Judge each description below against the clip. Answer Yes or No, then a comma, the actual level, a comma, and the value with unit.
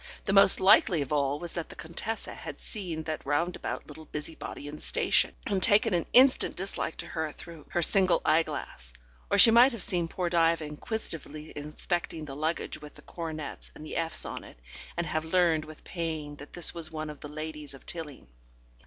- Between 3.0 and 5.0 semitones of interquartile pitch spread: No, narrow, 2.6 semitones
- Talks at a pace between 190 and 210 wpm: Yes, average, 195 wpm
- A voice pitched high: No, medium, 160 Hz